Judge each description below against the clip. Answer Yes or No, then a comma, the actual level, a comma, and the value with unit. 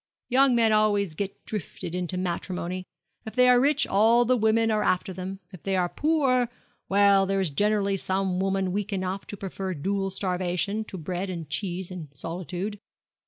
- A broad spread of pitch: No, average, 2.7 semitones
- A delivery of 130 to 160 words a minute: No, average, 175 wpm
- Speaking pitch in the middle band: No, high, 195 Hz